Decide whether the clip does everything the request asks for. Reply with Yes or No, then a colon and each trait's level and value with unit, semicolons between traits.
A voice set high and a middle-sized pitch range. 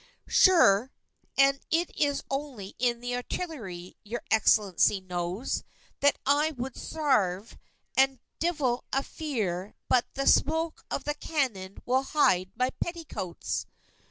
No: very high, 255 Hz; wide, 6.7 semitones